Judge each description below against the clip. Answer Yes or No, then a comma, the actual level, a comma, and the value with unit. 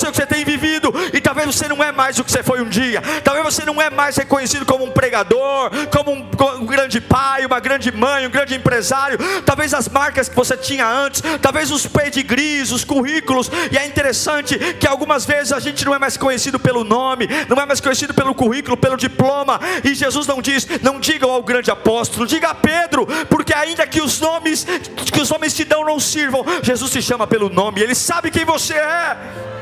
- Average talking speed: No, fast, 210 wpm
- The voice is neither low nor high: No, very high, 275 Hz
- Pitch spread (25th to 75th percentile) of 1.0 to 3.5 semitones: Yes, average, 2.7 semitones